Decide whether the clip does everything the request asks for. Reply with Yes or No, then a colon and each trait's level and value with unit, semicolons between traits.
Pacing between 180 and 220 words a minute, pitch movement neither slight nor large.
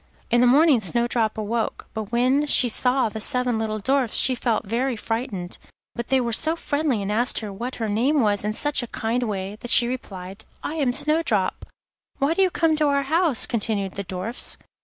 Yes: average, 200 wpm; average, 4.0 semitones